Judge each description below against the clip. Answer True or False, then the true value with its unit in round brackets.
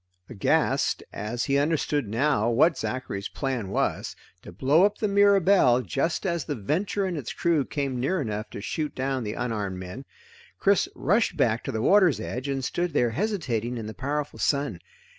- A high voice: False (135 Hz)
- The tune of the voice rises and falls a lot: True (6.7 semitones)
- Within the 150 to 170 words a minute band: False (180 wpm)